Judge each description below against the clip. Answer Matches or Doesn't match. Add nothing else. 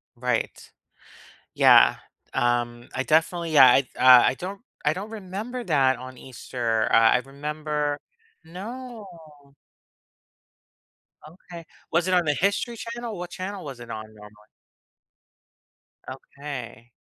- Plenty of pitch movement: Matches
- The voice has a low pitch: Doesn't match